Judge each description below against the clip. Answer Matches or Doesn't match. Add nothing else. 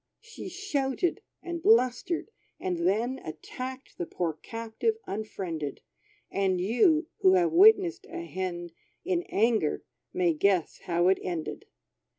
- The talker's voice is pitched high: Matches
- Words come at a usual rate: Doesn't match